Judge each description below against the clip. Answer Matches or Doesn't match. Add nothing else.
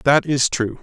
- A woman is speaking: Doesn't match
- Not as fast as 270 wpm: Matches